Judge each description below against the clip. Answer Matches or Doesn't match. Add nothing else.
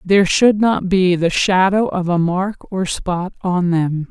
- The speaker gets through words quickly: Doesn't match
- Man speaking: Doesn't match